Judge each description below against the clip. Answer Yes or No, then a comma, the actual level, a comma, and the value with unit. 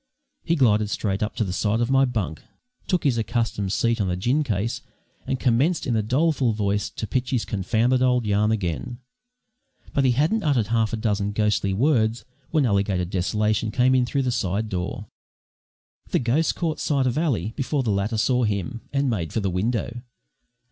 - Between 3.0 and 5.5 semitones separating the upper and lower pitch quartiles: Yes, average, 4.0 semitones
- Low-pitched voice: Yes, low, 115 Hz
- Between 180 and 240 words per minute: Yes, average, 190 wpm